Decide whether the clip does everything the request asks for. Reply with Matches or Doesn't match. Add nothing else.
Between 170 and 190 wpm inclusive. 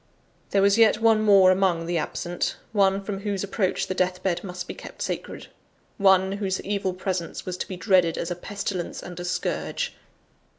Matches